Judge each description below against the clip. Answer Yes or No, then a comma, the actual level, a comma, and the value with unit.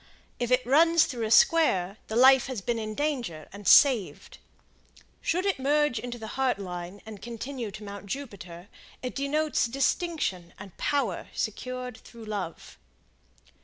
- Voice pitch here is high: Yes, high, 240 Hz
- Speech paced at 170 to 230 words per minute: No, average, 150 wpm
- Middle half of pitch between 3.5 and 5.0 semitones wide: No, wide, 5.4 semitones